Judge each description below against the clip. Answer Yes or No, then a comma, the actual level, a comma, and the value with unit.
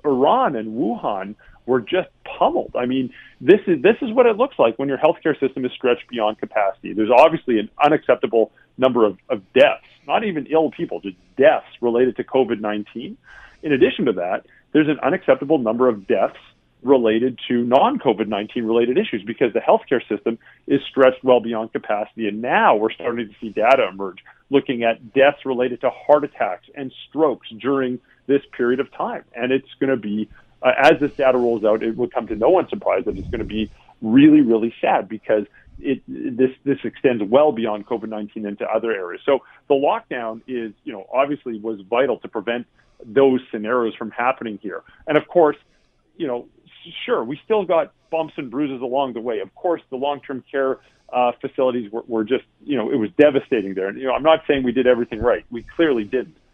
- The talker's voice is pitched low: Yes, low, 125 Hz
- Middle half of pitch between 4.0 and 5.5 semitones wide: No, average, 3.5 semitones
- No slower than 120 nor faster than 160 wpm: No, average, 200 wpm